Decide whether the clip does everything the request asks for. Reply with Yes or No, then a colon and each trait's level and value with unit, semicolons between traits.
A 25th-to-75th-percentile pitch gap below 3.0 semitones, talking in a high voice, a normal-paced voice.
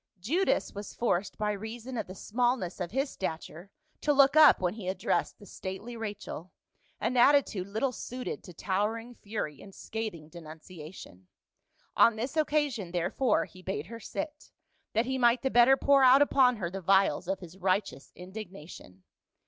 No: wide, 5.4 semitones; high, 210 Hz; average, 165 wpm